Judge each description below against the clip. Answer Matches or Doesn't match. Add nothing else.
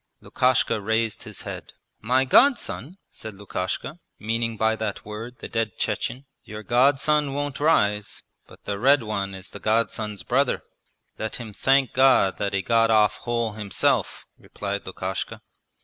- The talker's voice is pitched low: Matches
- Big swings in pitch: Doesn't match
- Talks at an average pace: Matches